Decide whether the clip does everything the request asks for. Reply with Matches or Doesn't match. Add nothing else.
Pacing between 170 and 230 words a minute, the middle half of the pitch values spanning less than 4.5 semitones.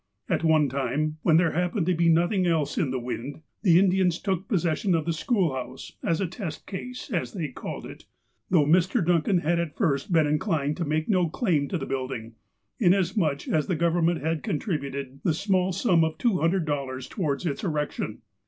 Matches